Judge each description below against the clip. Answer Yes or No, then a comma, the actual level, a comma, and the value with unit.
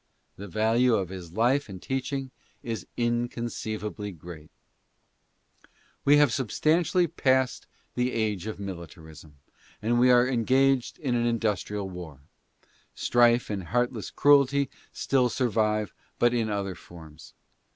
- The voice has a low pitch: Yes, low, 115 Hz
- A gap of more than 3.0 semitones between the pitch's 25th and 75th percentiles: Yes, average, 4.5 semitones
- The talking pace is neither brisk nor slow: No, slow, 130 wpm